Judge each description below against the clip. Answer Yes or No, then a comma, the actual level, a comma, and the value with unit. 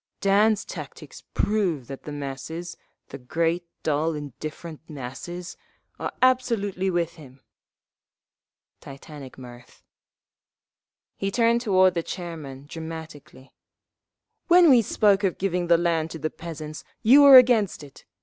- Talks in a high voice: No, medium, 170 Hz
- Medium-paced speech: No, slow, 115 wpm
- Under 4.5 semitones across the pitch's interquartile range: No, average, 5.1 semitones